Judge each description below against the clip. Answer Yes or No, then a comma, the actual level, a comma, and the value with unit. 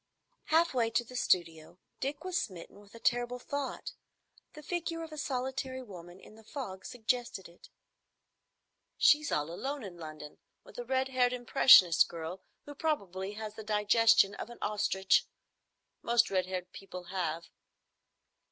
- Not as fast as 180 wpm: Yes, average, 150 wpm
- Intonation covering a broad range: Yes, wide, 5.8 semitones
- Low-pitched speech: No, high, 225 Hz